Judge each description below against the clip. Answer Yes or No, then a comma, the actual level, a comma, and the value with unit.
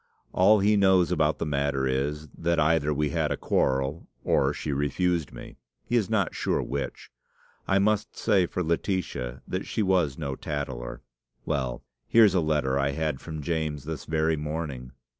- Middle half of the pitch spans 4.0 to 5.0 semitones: Yes, average, 4.4 semitones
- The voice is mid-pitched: No, very low, 80 Hz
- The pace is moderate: Yes, average, 170 wpm